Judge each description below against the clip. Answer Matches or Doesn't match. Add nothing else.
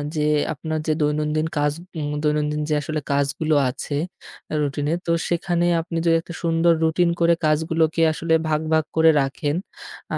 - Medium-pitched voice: Matches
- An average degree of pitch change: Doesn't match